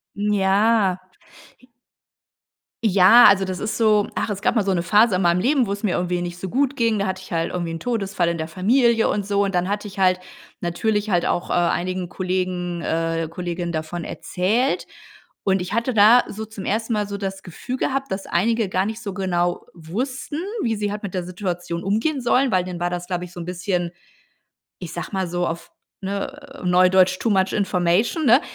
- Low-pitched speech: No, high, 190 Hz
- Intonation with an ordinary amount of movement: Yes, average, 3.6 semitones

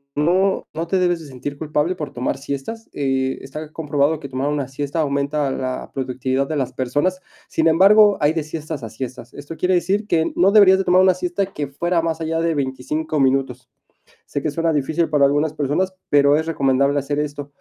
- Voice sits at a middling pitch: Yes, medium, 150 Hz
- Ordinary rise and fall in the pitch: Yes, average, 3.3 semitones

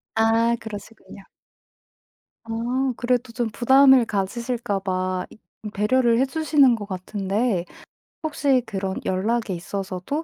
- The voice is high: Yes, high, 225 Hz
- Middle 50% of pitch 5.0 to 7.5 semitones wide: No, average, 4.3 semitones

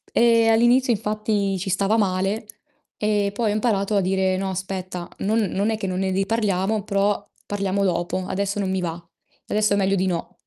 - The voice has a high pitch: Yes, high, 200 Hz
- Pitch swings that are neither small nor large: No, narrow, 2.1 semitones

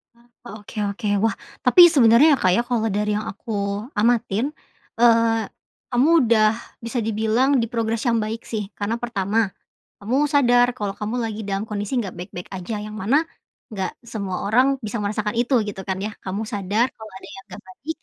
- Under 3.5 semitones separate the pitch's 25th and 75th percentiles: Yes, average, 2.8 semitones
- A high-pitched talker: Yes, high, 220 Hz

